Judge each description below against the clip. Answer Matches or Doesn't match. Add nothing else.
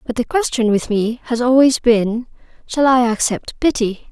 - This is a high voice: Matches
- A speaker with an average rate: Matches